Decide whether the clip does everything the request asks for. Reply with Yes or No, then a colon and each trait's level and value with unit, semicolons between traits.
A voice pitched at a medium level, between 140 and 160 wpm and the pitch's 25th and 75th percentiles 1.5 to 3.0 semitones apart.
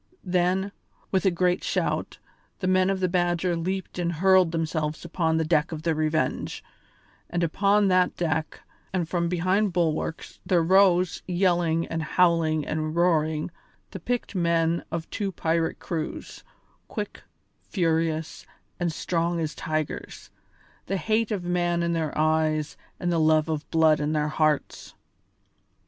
Yes: medium, 170 Hz; average, 145 wpm; narrow, 2.4 semitones